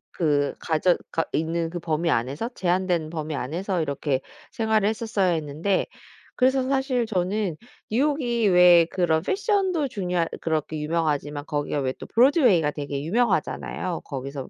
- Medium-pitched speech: Yes, medium, 175 Hz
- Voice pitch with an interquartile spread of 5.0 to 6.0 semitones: No, wide, 6.4 semitones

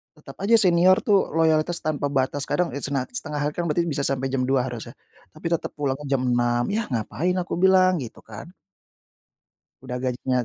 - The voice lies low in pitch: No, medium, 145 Hz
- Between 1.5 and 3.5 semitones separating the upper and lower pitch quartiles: No, average, 5.0 semitones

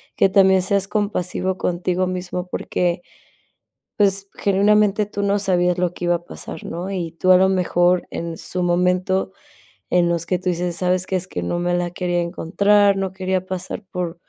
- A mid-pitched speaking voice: Yes, medium, 180 Hz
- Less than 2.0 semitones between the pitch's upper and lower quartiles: Yes, narrow, 1.5 semitones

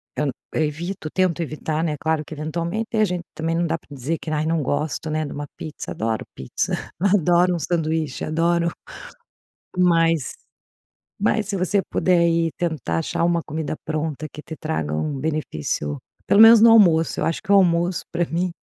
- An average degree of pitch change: No, narrow, 2.3 semitones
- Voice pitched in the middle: Yes, medium, 165 Hz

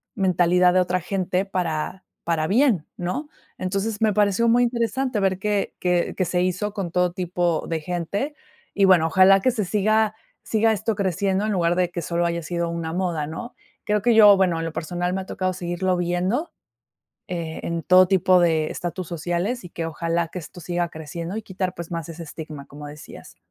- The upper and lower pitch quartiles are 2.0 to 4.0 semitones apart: Yes, average, 2.8 semitones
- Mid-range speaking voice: Yes, medium, 180 Hz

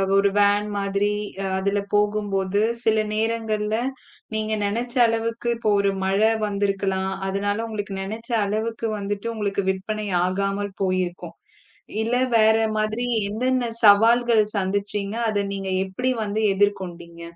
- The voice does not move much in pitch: Yes, narrow, 1.9 semitones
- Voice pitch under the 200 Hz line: No, high, 205 Hz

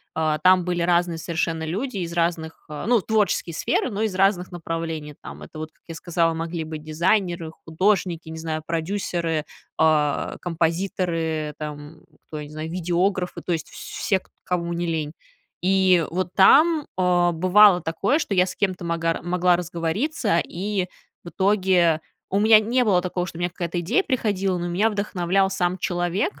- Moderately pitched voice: Yes, medium, 175 Hz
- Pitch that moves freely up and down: No, average, 2.7 semitones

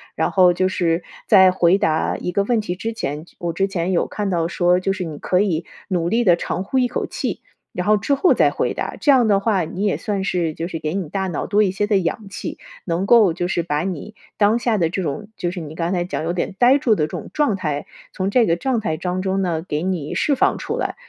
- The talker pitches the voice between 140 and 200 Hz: Yes, medium, 185 Hz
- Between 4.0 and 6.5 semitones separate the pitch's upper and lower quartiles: No, average, 3.4 semitones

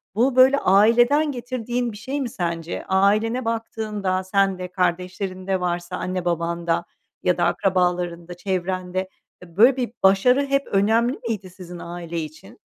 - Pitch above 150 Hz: Yes, high, 190 Hz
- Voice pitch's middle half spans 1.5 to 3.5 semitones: No, average, 4.4 semitones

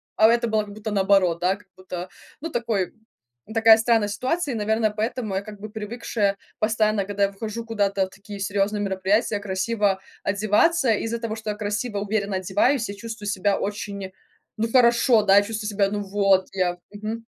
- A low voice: No, high, 210 Hz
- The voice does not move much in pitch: Yes, narrow, 2.1 semitones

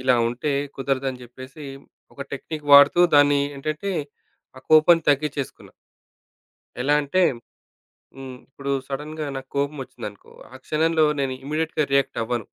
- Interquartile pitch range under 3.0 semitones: Yes, narrow, 2.4 semitones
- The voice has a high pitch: No, medium, 140 Hz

